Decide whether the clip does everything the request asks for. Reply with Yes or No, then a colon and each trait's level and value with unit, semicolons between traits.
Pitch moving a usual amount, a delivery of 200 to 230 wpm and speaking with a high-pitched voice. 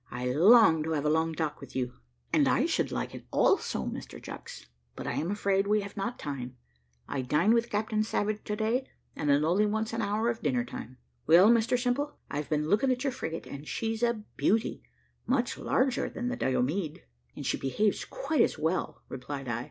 No: wide, 7.4 semitones; fast, 205 wpm; high, 200 Hz